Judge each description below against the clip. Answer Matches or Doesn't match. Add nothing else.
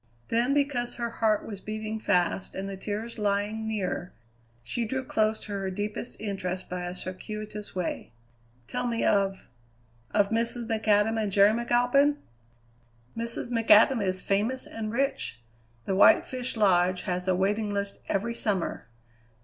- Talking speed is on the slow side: Doesn't match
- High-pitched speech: Matches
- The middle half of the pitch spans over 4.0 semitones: Doesn't match